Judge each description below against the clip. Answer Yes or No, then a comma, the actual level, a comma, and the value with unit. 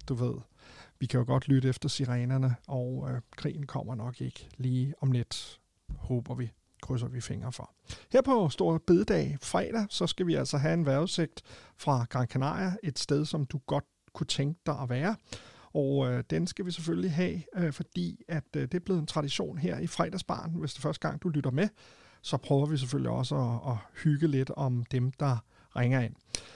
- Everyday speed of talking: Yes, average, 200 wpm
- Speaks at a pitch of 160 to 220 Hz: No, medium, 140 Hz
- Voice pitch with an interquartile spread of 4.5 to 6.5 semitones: Yes, average, 4.9 semitones